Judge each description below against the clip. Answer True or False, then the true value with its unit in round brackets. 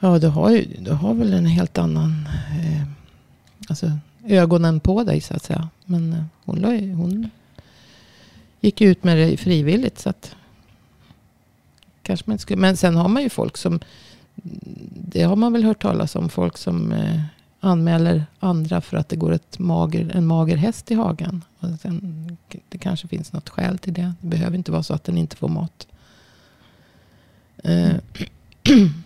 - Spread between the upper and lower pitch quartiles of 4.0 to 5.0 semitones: False (2.5 semitones)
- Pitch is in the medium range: True (175 Hz)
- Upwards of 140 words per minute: True (165 wpm)